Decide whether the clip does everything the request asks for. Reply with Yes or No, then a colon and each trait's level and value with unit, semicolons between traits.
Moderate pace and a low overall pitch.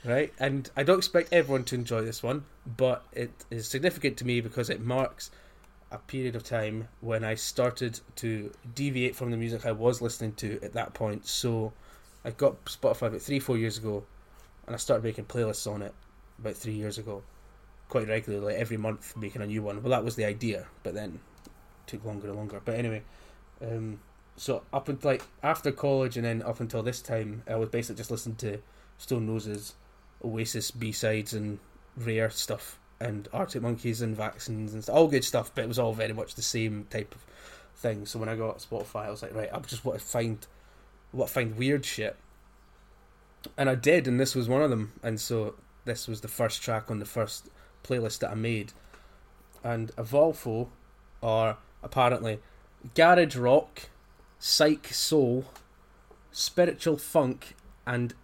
Yes: average, 185 wpm; low, 115 Hz